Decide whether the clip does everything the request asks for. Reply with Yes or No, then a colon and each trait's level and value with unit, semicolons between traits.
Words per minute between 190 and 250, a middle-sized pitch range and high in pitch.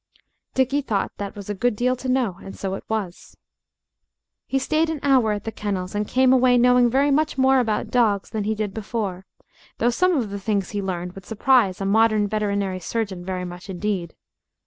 Yes: average, 200 wpm; average, 4.3 semitones; high, 215 Hz